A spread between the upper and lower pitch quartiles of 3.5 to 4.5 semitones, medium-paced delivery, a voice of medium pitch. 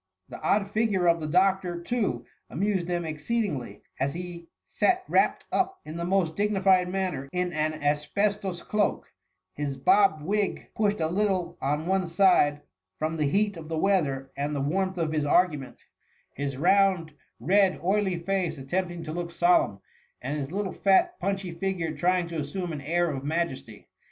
Yes: average, 4.2 semitones; average, 165 wpm; medium, 175 Hz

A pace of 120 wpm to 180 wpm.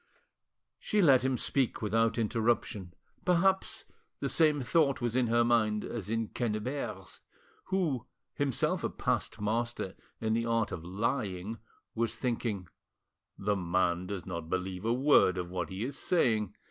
Yes: average, 145 wpm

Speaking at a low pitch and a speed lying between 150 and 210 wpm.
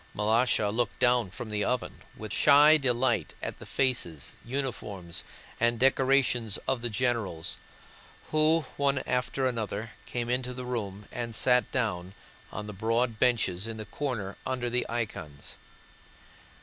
No: low, 120 Hz; average, 140 wpm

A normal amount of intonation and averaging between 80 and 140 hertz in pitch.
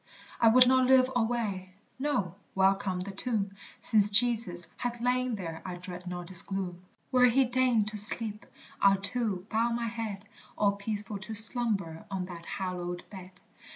No: average, 4.2 semitones; high, 205 Hz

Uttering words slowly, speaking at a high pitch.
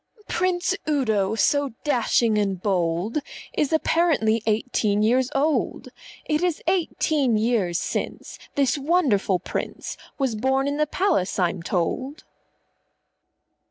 Yes: slow, 115 wpm; very high, 255 Hz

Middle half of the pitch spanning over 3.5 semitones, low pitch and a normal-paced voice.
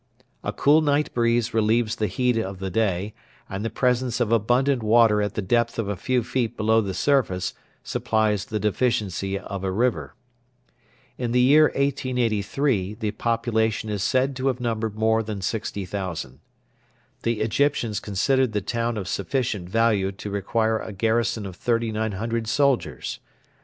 No: average, 2.9 semitones; low, 110 Hz; average, 155 wpm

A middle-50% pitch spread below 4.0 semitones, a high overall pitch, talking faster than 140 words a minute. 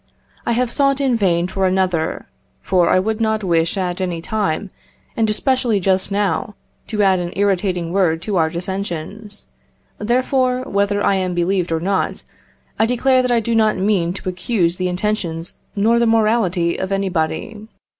Yes: average, 3.6 semitones; high, 195 Hz; average, 165 wpm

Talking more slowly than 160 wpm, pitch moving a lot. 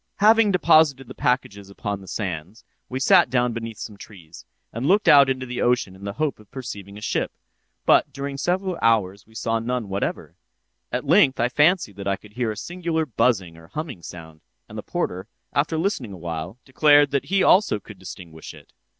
No: average, 195 wpm; wide, 6.6 semitones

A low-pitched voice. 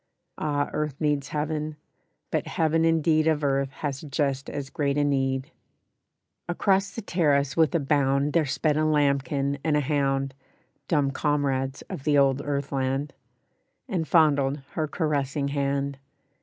No: medium, 145 Hz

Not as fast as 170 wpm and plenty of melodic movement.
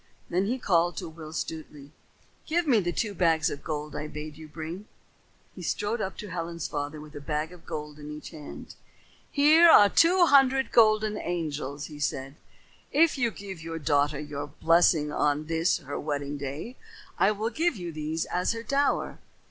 No: average, 180 wpm; wide, 6.0 semitones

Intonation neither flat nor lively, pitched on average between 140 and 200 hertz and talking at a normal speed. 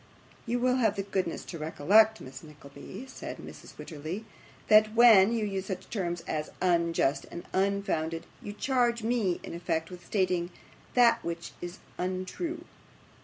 Yes: average, 4.6 semitones; high, 190 Hz; average, 150 wpm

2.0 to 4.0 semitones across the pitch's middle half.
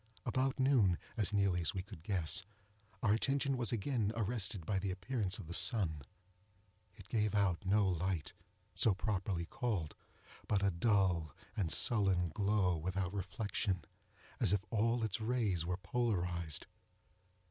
Yes: average, 3.6 semitones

